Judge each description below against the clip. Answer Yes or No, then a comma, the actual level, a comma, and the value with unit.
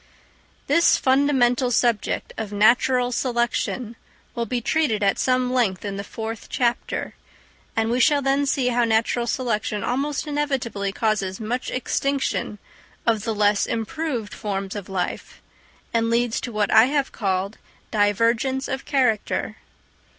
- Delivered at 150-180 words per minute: No, slow, 135 wpm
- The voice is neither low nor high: No, high, 235 Hz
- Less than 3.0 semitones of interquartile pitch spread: No, average, 3.5 semitones